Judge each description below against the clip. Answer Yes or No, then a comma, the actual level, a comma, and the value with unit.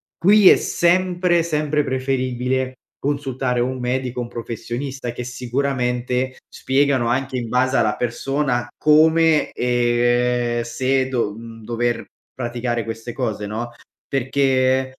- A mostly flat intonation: Yes, narrow, 2.2 semitones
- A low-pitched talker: Yes, low, 130 Hz